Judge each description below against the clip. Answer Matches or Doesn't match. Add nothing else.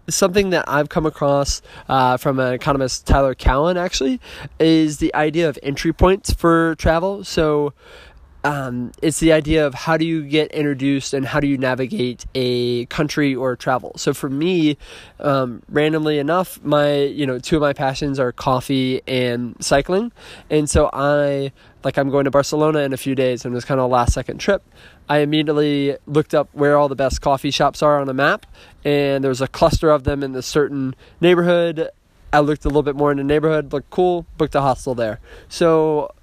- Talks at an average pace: Matches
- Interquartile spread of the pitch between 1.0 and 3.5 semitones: Matches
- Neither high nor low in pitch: Matches